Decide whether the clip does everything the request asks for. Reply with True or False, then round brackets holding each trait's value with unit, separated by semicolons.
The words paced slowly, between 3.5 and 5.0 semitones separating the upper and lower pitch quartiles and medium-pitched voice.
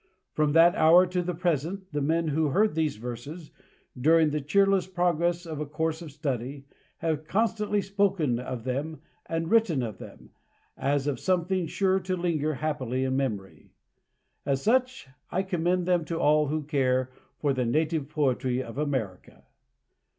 False (160 wpm; 4.4 semitones; 155 Hz)